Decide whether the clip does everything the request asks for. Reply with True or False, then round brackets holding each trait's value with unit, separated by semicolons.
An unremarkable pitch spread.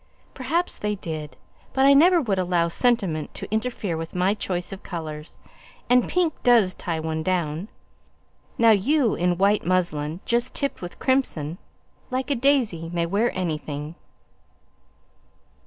False (6.9 semitones)